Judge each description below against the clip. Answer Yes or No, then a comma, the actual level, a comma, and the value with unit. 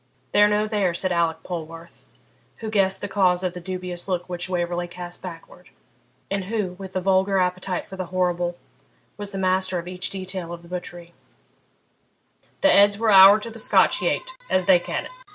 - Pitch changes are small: Yes, narrow, 1.8 semitones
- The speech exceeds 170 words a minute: Yes, average, 180 wpm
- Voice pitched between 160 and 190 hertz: Yes, medium, 185 Hz